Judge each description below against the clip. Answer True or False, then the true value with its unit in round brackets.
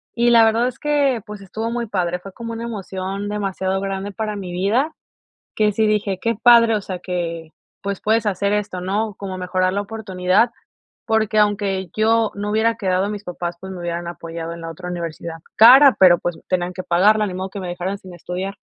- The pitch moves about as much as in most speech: True (3.2 semitones)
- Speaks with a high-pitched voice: True (195 Hz)